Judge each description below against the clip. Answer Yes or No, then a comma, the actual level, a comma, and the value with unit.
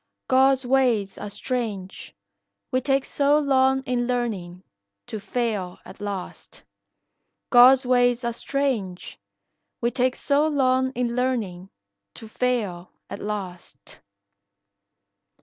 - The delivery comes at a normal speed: No, slow, 110 wpm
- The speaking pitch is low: No, high, 245 Hz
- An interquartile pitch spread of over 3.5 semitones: Yes, average, 4.3 semitones